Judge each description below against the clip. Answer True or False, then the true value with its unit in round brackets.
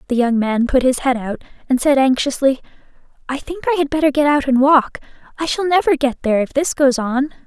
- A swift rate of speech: True (225 wpm)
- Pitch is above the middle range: True (270 Hz)